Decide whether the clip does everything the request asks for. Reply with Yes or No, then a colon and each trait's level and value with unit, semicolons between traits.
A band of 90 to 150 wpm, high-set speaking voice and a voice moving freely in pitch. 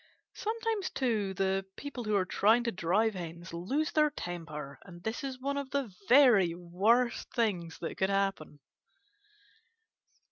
Yes: average, 145 wpm; high, 205 Hz; wide, 6.6 semitones